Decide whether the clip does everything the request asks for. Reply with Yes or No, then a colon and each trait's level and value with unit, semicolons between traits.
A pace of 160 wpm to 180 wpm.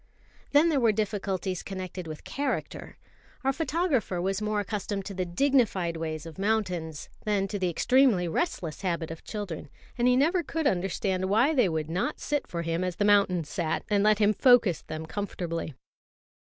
Yes: average, 175 wpm